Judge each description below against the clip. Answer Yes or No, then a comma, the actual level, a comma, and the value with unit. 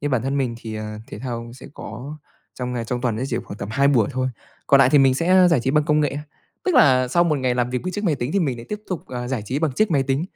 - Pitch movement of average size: Yes, average, 3.6 semitones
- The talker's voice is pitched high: No, low, 130 Hz